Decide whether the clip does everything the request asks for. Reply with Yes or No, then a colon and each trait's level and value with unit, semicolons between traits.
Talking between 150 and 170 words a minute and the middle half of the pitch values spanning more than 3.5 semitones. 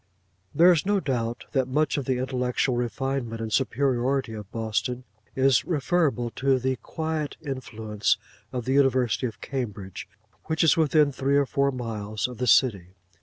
No: average, 160 wpm; average, 3.2 semitones